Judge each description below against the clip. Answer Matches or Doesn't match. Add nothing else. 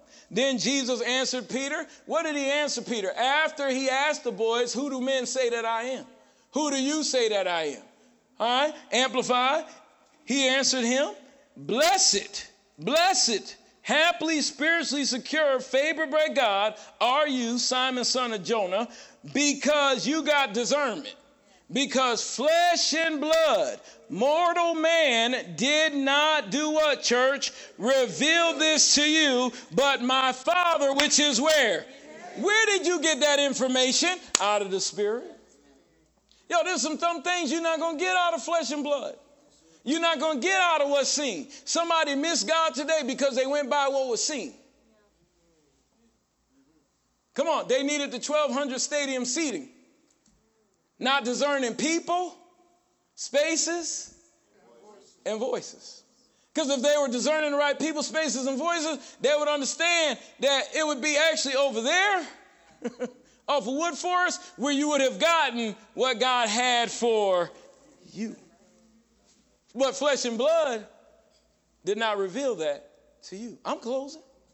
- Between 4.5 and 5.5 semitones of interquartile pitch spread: Doesn't match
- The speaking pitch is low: Doesn't match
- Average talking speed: Matches